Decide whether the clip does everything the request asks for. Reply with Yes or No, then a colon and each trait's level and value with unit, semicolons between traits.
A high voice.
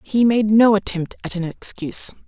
Yes: high, 205 Hz